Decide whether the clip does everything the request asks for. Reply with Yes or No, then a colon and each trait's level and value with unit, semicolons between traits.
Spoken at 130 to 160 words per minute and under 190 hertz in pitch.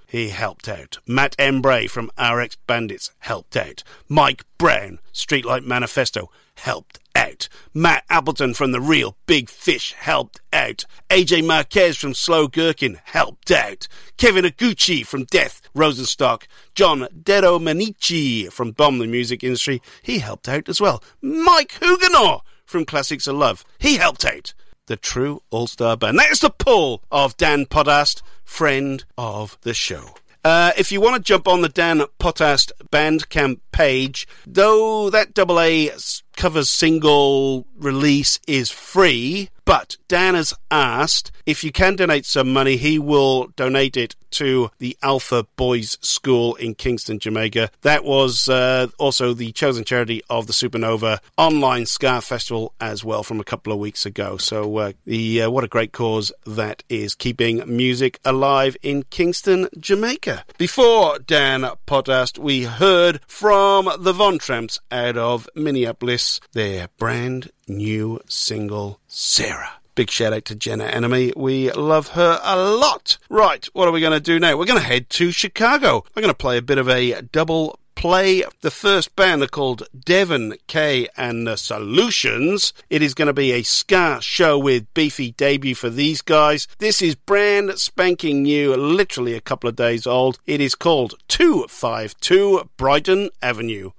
Yes: average, 155 wpm; low, 135 Hz